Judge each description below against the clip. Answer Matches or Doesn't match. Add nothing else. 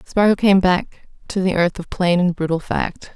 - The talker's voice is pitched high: Doesn't match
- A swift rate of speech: Matches